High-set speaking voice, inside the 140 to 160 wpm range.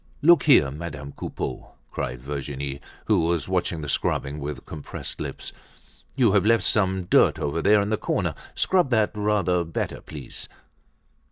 No: very low, 85 Hz; average, 155 wpm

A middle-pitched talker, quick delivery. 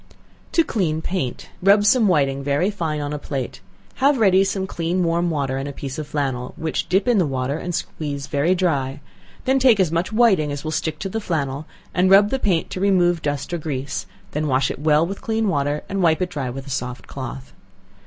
Yes: medium, 160 Hz; fast, 220 wpm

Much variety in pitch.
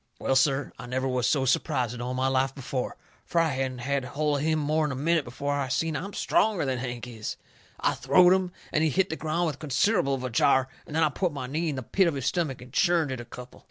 No: average, 3.7 semitones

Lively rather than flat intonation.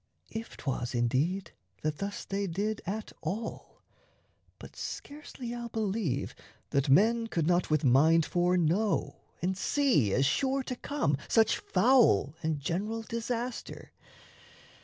Yes: wide, 6.8 semitones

